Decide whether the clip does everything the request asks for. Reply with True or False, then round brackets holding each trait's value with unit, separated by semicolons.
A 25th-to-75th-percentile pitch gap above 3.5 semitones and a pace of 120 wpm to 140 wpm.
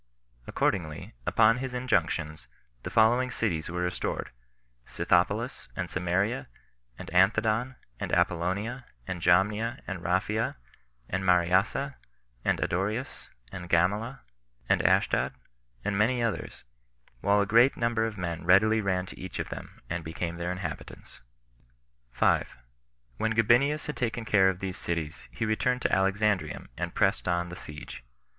True (4.3 semitones; 135 wpm)